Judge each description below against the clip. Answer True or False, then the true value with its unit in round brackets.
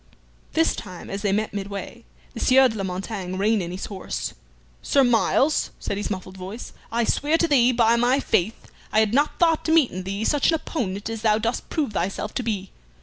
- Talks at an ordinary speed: False (210 wpm)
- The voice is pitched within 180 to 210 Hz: False (220 Hz)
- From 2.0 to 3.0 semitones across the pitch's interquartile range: False (4.6 semitones)